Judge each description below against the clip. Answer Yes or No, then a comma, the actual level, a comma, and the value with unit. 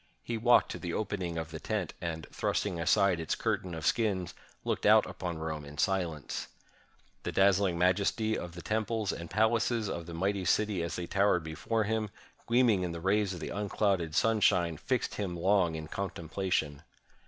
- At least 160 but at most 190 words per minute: Yes, average, 180 wpm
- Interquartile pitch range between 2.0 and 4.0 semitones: Yes, average, 3.7 semitones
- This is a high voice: No, very low, 95 Hz